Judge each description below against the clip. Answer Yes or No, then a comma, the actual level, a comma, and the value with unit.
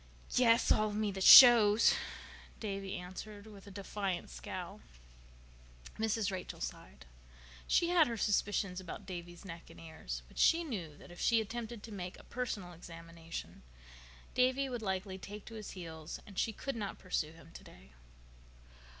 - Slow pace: No, average, 155 wpm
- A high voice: Yes, high, 200 Hz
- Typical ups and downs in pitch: Yes, average, 4.2 semitones